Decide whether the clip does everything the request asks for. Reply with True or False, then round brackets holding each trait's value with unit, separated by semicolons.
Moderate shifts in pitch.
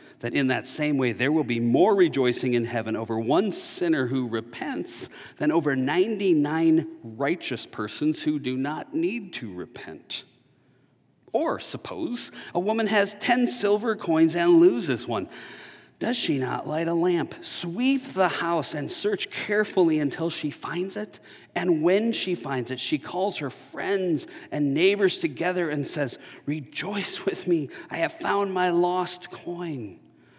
False (5.7 semitones)